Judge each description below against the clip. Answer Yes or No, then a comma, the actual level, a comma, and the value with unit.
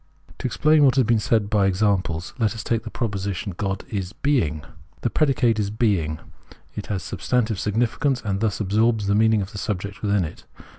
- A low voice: Yes, low, 105 Hz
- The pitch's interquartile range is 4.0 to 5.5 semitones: No, average, 2.9 semitones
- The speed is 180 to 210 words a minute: Yes, average, 200 wpm